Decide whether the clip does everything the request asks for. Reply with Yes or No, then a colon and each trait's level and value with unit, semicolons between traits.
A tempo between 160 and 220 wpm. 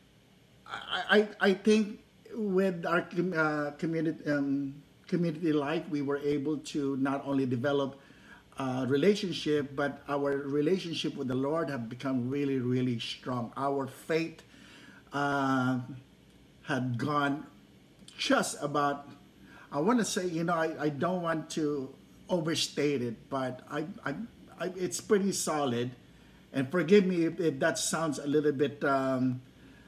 No: slow, 135 wpm